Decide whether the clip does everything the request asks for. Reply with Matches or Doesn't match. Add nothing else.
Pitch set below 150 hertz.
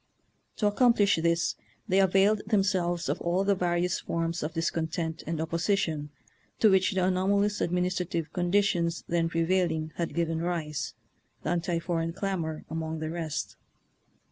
Doesn't match